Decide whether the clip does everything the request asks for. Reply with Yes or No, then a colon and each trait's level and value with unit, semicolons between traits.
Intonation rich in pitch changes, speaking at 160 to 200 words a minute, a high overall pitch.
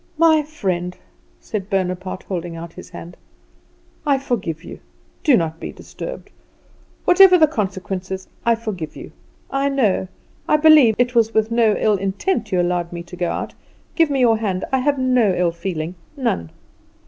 Yes: wide, 6.7 semitones; average, 170 wpm; high, 205 Hz